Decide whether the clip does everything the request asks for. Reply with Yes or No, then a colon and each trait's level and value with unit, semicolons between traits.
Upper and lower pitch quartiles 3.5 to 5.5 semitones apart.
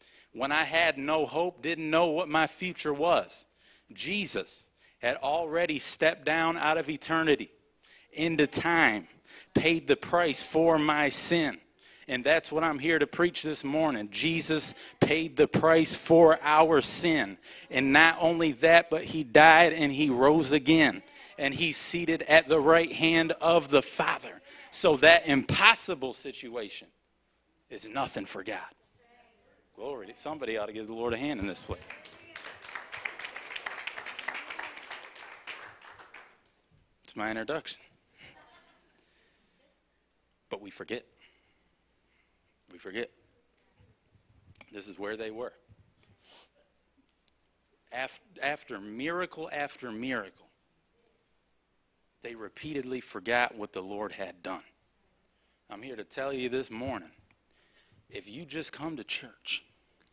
No: average, 3.1 semitones